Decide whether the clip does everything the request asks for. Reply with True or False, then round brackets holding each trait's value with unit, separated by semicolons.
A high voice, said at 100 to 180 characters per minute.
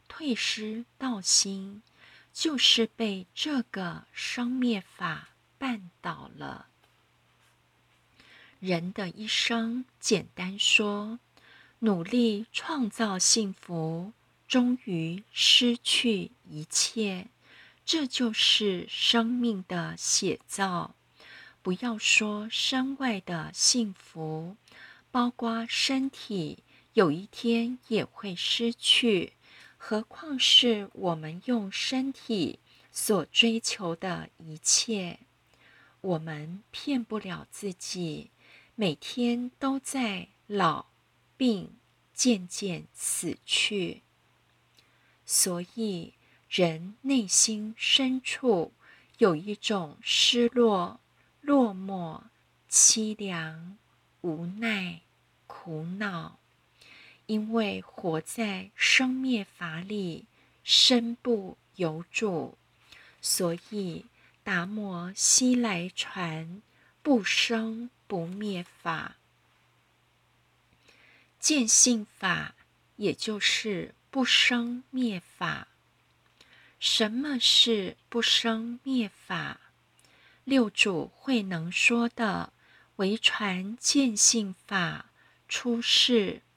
True (215 Hz; 115 characters per minute)